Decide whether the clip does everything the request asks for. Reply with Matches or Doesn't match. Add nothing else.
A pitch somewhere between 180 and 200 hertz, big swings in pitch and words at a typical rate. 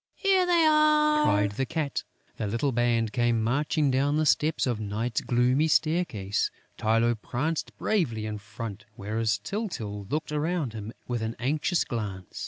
Doesn't match